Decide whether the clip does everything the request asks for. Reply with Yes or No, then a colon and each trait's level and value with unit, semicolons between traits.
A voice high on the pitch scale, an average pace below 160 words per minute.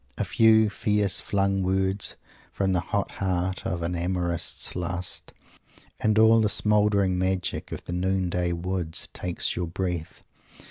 No: very low, 95 Hz; average, 145 wpm